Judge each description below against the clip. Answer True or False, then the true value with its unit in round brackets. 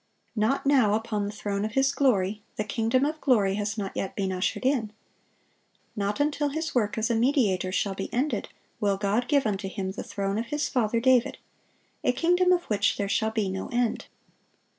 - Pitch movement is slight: False (4.6 semitones)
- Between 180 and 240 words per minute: True (195 wpm)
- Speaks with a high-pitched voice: True (220 Hz)